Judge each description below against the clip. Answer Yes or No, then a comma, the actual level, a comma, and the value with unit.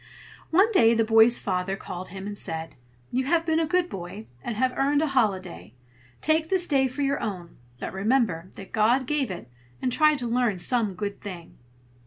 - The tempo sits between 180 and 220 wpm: Yes, average, 195 wpm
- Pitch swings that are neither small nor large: No, wide, 6.5 semitones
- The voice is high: Yes, high, 230 Hz